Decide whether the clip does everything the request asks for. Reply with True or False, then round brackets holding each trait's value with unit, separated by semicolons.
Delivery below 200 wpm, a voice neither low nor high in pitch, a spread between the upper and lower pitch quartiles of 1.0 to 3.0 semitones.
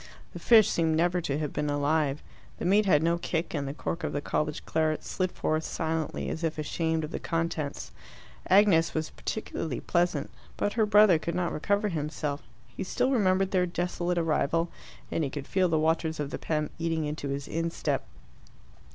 True (185 wpm; 165 Hz; 2.7 semitones)